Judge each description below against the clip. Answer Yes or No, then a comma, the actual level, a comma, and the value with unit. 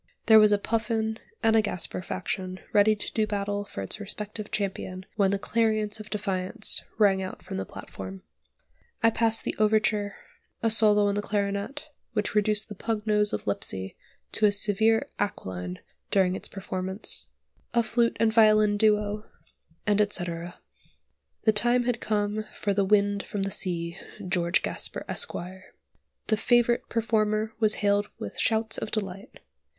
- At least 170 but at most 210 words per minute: No, average, 155 wpm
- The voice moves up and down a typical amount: No, narrow, 1.9 semitones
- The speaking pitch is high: Yes, high, 210 Hz